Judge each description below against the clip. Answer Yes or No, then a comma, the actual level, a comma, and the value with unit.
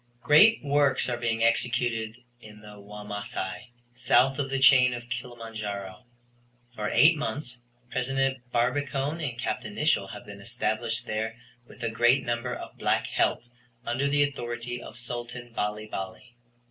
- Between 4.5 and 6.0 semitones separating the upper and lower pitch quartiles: No, average, 3.0 semitones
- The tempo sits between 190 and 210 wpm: No, average, 145 wpm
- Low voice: Yes, low, 120 Hz